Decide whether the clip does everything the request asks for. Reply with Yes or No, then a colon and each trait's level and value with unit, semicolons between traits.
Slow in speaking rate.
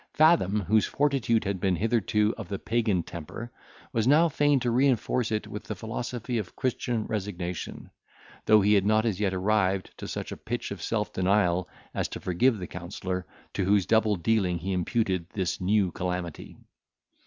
No: average, 175 wpm